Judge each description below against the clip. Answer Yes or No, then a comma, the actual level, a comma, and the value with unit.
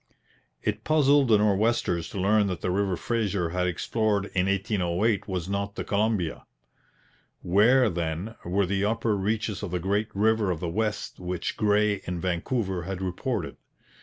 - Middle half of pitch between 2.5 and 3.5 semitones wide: Yes, average, 3.1 semitones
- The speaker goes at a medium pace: Yes, average, 160 wpm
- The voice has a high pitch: No, low, 100 Hz